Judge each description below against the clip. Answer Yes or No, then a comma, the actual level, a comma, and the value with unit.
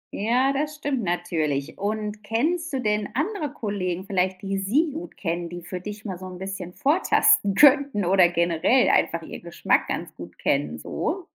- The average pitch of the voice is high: Yes, high, 205 Hz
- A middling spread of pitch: No, wide, 7.2 semitones